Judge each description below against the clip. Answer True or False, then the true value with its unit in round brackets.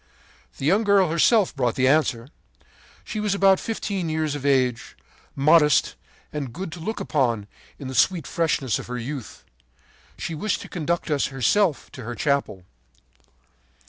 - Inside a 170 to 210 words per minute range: False (155 wpm)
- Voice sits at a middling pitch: True (150 Hz)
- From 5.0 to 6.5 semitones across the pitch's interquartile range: True (5.6 semitones)